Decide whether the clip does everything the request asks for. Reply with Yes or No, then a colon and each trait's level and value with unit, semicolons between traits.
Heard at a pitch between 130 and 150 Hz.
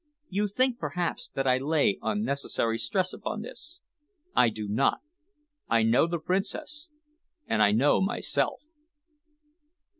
No: medium, 160 Hz